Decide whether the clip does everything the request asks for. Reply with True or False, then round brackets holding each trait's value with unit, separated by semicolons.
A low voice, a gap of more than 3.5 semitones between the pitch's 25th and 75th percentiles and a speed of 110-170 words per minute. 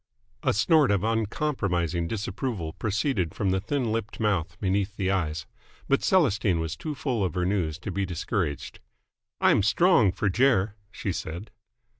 True (100 Hz; 4.2 semitones; 155 wpm)